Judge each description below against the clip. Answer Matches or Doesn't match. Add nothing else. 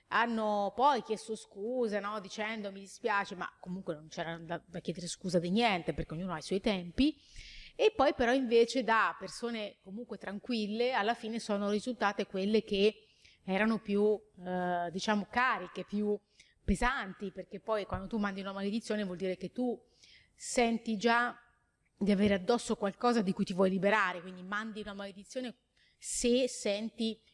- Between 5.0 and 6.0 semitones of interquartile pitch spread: Doesn't match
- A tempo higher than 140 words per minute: Matches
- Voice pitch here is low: Doesn't match